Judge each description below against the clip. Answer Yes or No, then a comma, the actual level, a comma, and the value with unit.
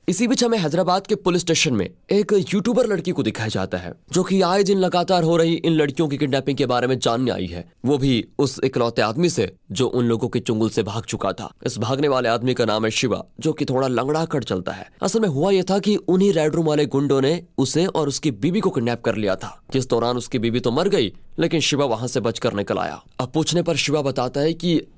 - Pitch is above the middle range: No, medium, 140 Hz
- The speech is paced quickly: Yes, fast, 250 wpm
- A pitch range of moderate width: No, wide, 6.6 semitones